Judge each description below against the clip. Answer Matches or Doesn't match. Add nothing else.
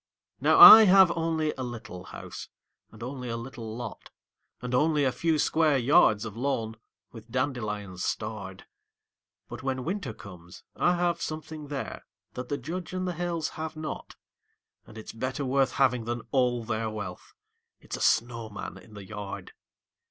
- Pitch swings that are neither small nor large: Doesn't match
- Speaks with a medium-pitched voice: Doesn't match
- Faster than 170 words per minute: Doesn't match